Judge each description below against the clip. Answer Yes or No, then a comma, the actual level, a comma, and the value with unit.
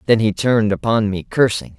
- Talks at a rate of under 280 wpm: Yes, average, 200 wpm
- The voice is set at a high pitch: No, low, 110 Hz